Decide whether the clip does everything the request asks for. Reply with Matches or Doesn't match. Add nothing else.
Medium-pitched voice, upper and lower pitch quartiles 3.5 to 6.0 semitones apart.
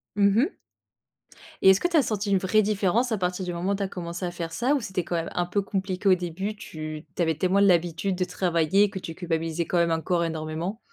Doesn't match